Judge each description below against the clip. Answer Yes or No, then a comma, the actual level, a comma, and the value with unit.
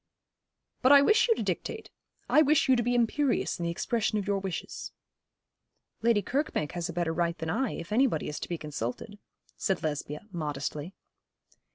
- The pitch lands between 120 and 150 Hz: No, high, 195 Hz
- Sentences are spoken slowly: No, average, 180 wpm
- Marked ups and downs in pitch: Yes, wide, 7.1 semitones